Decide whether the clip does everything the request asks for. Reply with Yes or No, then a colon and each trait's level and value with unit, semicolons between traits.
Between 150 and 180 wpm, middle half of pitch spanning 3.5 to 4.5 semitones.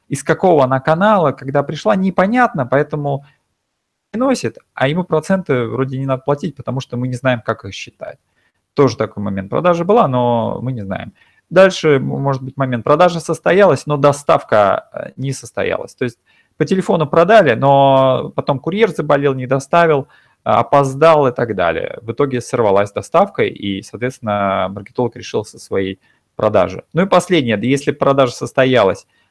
No: average, 155 wpm; average, 5.1 semitones